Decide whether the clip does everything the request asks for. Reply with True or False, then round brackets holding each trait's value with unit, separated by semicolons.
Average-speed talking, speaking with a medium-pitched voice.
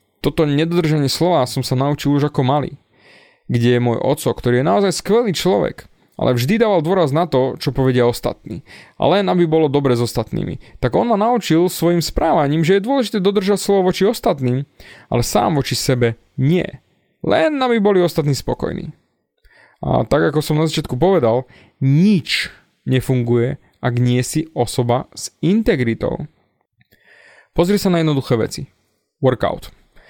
True (155 wpm; 145 Hz)